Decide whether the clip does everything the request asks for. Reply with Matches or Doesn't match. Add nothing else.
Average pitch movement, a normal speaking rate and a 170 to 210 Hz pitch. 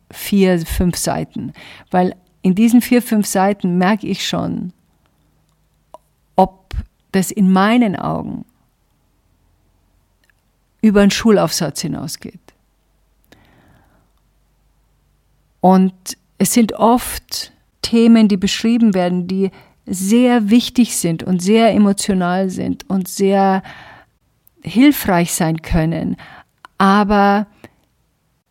Doesn't match